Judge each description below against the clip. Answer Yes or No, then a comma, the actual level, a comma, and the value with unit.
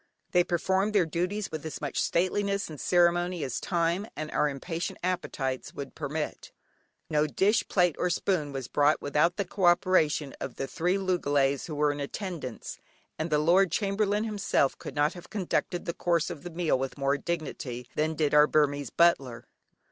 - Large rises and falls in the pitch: No, average, 3.8 semitones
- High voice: No, medium, 165 Hz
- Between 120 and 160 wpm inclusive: No, average, 180 wpm